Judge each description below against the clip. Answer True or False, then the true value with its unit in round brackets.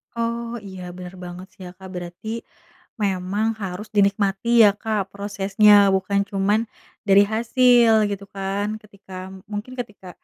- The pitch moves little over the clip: True (2.1 semitones)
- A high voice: True (200 Hz)